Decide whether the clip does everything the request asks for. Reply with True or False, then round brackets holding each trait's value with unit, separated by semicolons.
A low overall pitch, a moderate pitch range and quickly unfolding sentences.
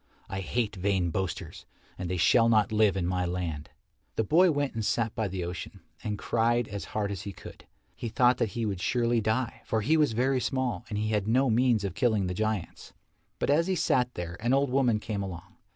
True (110 Hz; 4.1 semitones; 220 wpm)